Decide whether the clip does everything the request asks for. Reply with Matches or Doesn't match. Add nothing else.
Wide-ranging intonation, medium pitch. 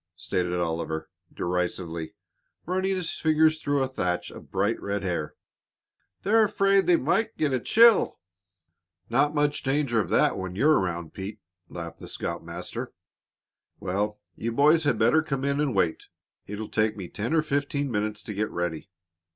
Doesn't match